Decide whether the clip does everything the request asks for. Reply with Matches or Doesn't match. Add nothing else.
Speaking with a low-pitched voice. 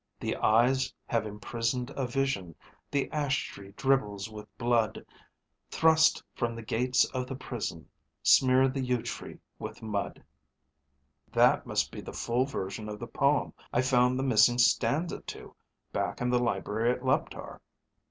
Matches